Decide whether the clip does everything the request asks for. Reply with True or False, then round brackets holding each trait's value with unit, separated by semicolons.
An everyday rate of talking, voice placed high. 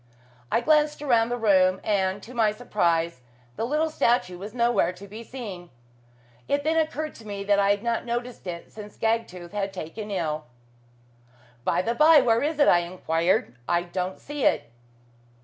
True (180 wpm; 210 Hz)